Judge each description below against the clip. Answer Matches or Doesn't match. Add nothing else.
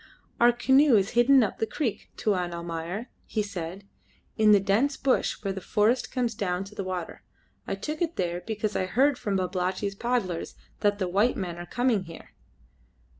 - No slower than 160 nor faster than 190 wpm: Matches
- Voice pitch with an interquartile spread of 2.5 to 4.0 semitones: Doesn't match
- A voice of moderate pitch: Doesn't match